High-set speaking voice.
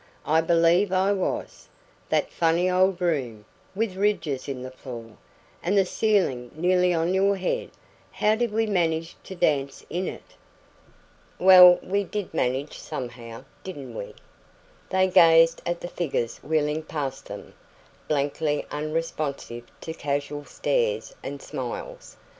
No: medium, 165 Hz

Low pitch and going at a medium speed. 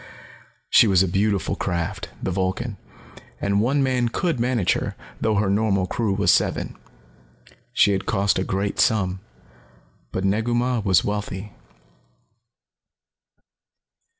No: low, 100 Hz; slow, 125 wpm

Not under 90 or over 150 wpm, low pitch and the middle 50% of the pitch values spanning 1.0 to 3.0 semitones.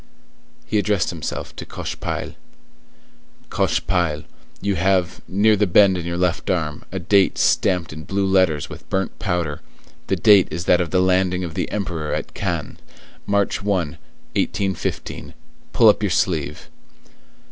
Yes: average, 145 wpm; very low, 90 Hz; narrow, 2.6 semitones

